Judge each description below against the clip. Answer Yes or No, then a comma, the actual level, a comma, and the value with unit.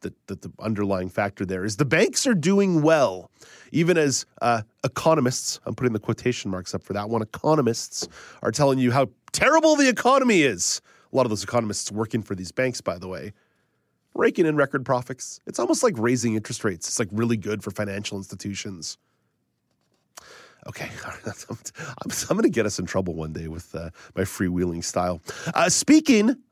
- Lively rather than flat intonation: Yes, wide, 6.6 semitones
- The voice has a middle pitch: No, low, 115 Hz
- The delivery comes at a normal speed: Yes, average, 175 wpm